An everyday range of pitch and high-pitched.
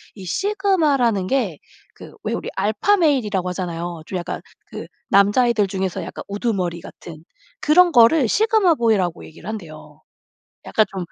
No: wide, 7.5 semitones; high, 210 Hz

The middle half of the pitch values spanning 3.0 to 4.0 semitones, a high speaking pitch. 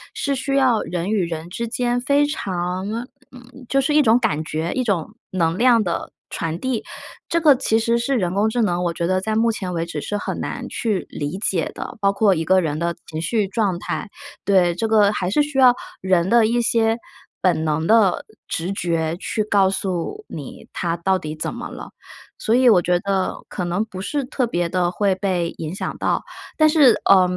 No: average, 5.1 semitones; high, 195 Hz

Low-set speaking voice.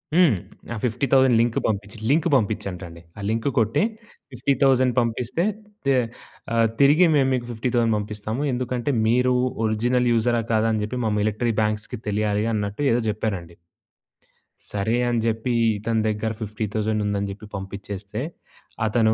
Yes: low, 110 Hz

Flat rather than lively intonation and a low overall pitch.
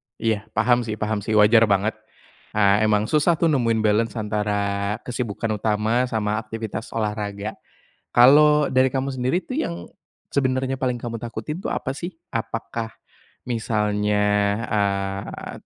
No: average, 3.1 semitones; low, 110 Hz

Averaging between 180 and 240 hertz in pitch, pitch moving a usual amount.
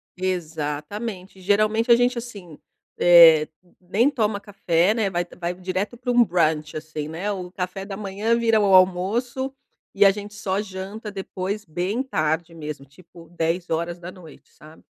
Yes: medium, 185 Hz; average, 3.7 semitones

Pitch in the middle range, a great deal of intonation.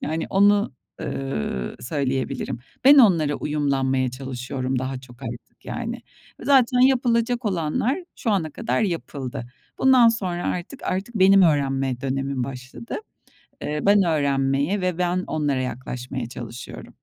Yes: medium, 150 Hz; wide, 7.0 semitones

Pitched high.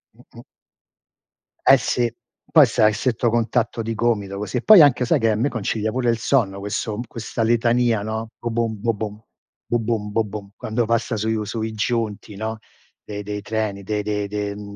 No: low, 110 Hz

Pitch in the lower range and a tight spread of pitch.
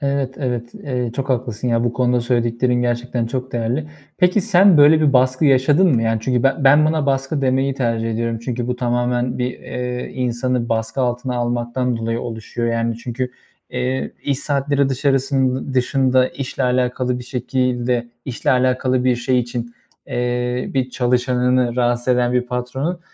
Yes: low, 125 Hz; narrow, 1.6 semitones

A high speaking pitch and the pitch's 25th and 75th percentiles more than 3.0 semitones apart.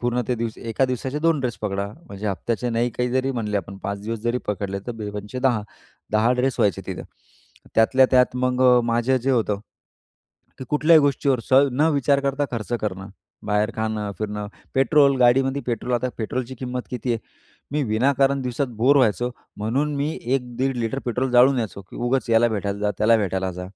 No: low, 120 Hz; average, 3.6 semitones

